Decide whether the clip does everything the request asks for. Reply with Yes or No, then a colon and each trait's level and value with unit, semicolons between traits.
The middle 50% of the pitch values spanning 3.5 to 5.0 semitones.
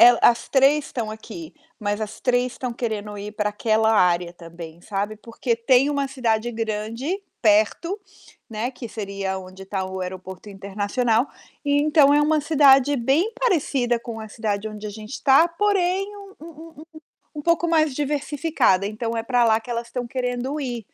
No: wide, 5.4 semitones